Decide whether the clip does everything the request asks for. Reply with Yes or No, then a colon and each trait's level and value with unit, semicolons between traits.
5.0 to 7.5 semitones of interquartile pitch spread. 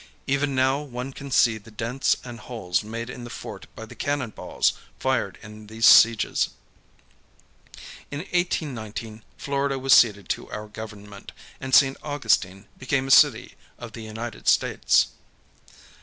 No: average, 3.8 semitones